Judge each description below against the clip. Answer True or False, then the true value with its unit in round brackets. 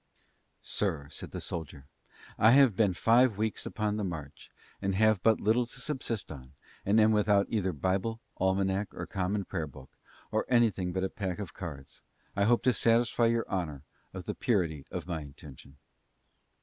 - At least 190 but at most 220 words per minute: False (175 wpm)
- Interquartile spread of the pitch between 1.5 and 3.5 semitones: False (4.5 semitones)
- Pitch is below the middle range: True (100 Hz)